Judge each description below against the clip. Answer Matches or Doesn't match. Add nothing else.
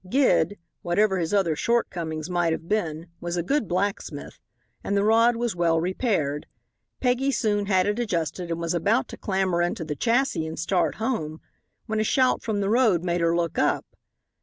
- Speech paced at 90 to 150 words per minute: Doesn't match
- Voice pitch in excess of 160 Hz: Matches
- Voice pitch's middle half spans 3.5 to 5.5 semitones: Matches